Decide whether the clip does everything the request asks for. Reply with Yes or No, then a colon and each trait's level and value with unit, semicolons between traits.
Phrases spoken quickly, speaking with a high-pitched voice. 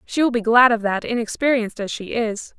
Yes: fast, 230 wpm; high, 230 Hz